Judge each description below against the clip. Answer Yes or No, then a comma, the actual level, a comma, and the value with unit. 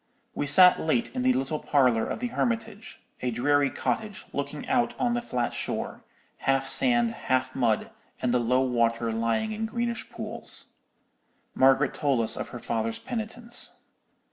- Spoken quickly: No, average, 160 wpm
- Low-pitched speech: No, medium, 145 Hz